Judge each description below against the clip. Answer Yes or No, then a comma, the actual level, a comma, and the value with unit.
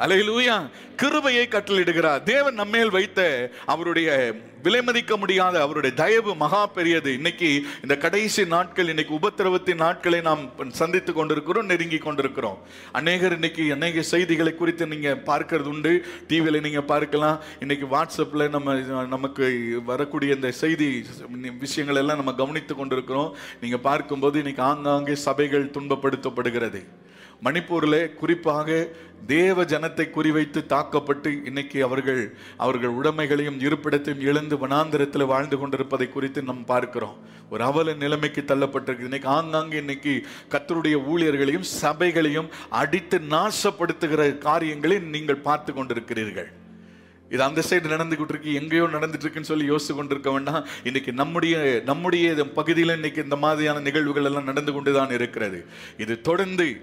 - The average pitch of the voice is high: No, medium, 150 Hz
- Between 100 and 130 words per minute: Yes, average, 120 wpm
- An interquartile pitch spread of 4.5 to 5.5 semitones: No, average, 3.1 semitones